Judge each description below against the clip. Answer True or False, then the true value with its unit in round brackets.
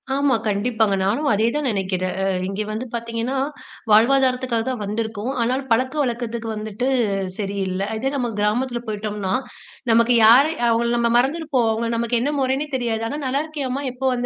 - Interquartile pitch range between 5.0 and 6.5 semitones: False (3.3 semitones)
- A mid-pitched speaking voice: False (235 Hz)